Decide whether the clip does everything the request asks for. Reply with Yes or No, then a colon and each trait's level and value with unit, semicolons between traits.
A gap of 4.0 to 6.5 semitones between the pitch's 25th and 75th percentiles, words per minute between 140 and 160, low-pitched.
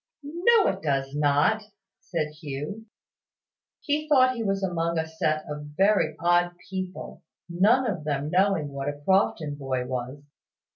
No: wide, 5.6 semitones; average, 145 wpm; medium, 165 Hz